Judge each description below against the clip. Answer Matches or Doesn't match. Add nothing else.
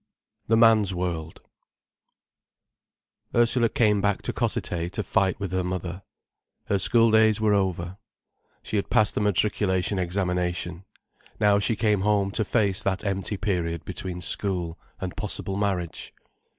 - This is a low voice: Matches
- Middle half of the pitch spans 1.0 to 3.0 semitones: Matches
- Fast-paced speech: Doesn't match